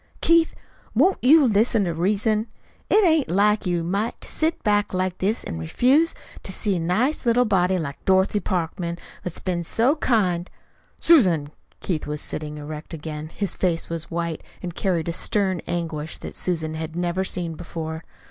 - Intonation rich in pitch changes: No, average, 4.5 semitones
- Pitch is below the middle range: No, medium, 180 Hz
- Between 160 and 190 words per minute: Yes, average, 175 wpm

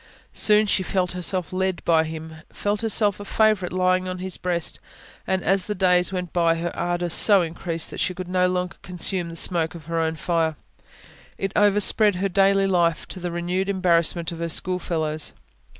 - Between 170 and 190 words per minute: Yes, average, 185 wpm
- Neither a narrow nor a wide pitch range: No, narrow, 2.1 semitones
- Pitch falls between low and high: Yes, medium, 180 Hz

